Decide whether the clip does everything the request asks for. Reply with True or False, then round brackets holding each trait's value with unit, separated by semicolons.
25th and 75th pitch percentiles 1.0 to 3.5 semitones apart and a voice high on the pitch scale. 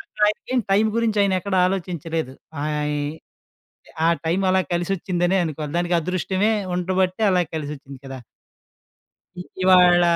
False (2.9 semitones; 180 Hz)